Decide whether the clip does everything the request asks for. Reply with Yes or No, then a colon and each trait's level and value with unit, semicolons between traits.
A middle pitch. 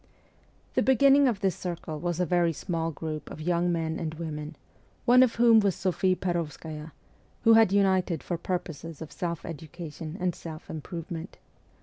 Yes: medium, 170 Hz